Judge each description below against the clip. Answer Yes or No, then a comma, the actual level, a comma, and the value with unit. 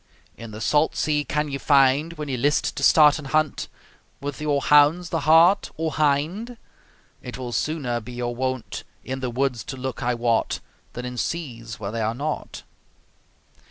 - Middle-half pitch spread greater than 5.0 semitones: No, average, 3.8 semitones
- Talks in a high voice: No, medium, 140 Hz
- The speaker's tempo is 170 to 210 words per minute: Yes, average, 180 wpm